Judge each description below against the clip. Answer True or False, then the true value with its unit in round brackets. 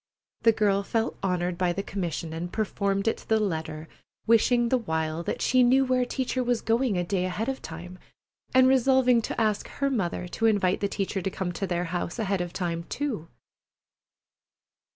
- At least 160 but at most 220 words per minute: True (190 wpm)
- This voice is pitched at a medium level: False (200 Hz)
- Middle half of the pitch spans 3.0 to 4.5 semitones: False (5.2 semitones)